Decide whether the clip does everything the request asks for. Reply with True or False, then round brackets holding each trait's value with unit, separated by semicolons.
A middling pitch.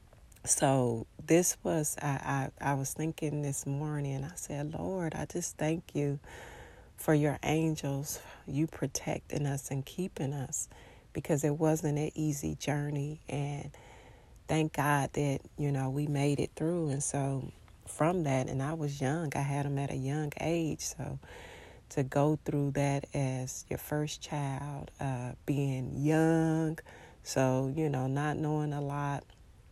True (145 Hz)